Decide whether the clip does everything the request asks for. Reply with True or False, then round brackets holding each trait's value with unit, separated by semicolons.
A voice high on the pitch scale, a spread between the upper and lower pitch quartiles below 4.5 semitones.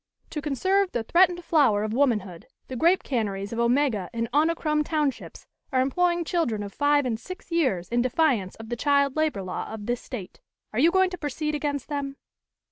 False (275 Hz; 5.6 semitones)